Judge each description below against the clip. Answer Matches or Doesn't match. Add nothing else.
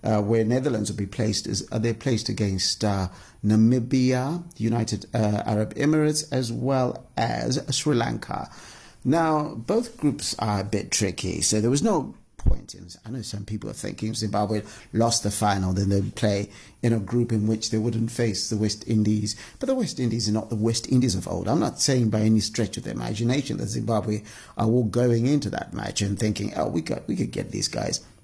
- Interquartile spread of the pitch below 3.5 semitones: Matches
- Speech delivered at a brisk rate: Matches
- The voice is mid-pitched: Doesn't match